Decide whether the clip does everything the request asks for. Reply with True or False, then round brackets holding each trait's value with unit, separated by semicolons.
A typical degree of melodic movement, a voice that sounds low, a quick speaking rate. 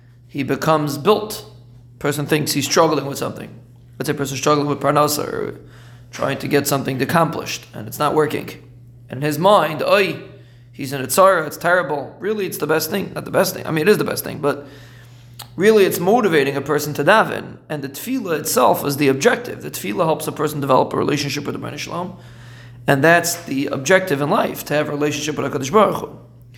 False (3.1 semitones; 145 Hz; 210 wpm)